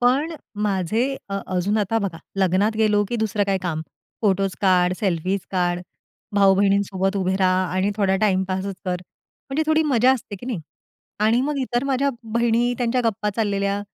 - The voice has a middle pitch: No, high, 200 Hz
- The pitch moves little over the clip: No, average, 3.7 semitones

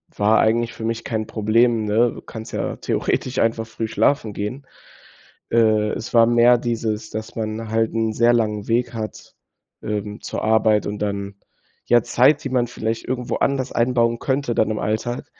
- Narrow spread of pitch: Yes, narrow, 1.7 semitones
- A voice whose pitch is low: Yes, low, 115 Hz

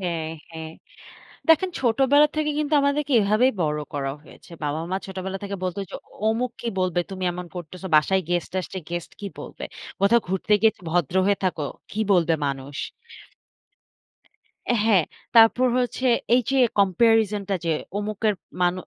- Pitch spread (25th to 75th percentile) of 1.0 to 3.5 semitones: No, average, 4.7 semitones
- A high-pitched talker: Yes, high, 195 Hz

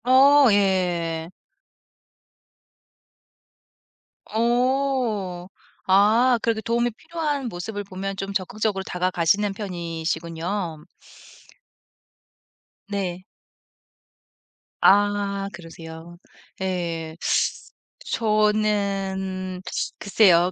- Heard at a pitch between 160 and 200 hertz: Yes, high, 195 Hz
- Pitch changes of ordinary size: Yes, average, 3.5 semitones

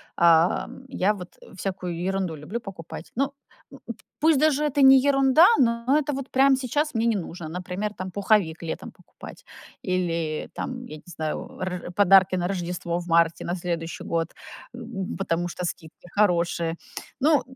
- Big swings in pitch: Yes, wide, 5.8 semitones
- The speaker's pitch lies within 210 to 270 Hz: No, medium, 185 Hz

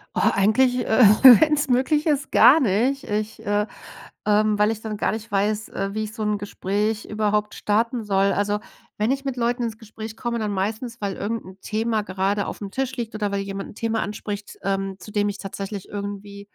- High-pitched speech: Yes, high, 210 Hz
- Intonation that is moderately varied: No, narrow, 2.2 semitones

